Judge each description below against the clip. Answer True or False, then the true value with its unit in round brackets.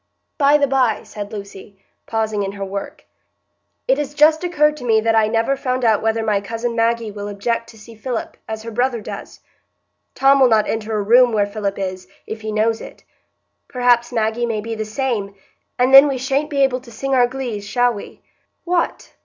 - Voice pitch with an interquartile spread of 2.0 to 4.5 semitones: True (3.3 semitones)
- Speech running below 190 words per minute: False (205 wpm)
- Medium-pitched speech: False (230 Hz)